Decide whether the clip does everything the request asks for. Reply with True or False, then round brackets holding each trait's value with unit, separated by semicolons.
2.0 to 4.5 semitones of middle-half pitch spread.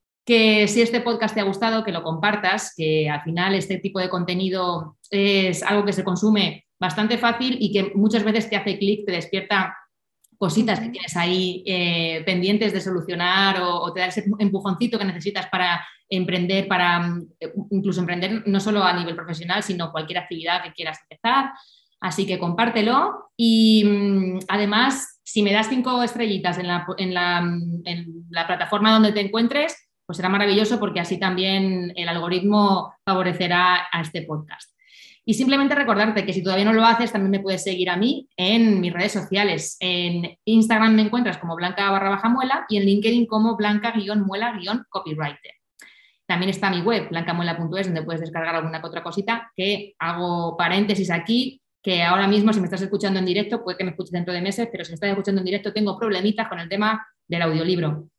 True (3.3 semitones)